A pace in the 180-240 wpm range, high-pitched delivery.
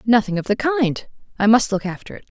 Yes: average, 200 wpm; high, 210 Hz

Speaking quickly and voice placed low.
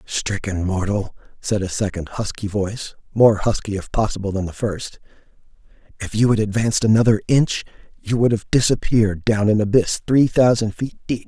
No: average, 165 wpm; low, 105 Hz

